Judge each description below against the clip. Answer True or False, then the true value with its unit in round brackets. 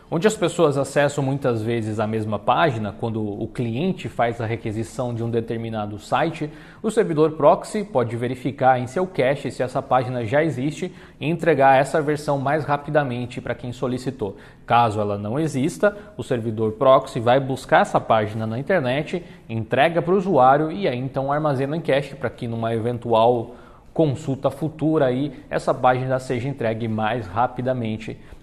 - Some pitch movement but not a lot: True (4.4 semitones)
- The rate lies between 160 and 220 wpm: True (165 wpm)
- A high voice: False (130 Hz)